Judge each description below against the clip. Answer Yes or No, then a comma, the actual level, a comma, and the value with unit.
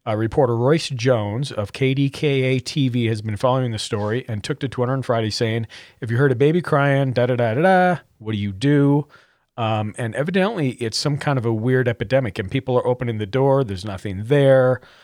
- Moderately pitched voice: No, low, 125 Hz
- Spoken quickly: No, average, 195 wpm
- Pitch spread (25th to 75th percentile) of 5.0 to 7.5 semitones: No, average, 3.4 semitones